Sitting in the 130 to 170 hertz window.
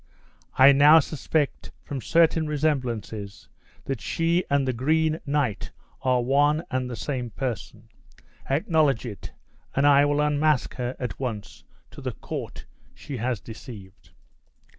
Yes: low, 135 Hz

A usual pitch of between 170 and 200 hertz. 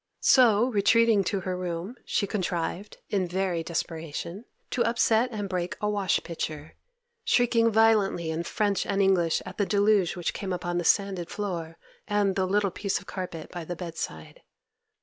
Yes: high, 190 Hz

